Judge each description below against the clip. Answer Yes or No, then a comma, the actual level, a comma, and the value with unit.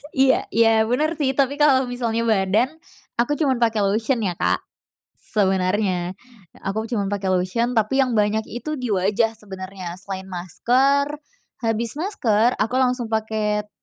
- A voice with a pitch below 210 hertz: No, high, 225 Hz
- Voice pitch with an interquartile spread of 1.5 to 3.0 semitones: No, average, 4.1 semitones